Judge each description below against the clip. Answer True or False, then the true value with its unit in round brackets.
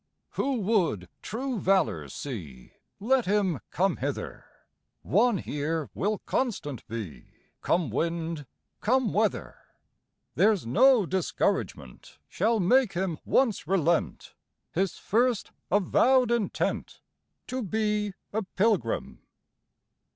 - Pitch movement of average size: False (5.9 semitones)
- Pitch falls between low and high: False (195 Hz)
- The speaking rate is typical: False (100 wpm)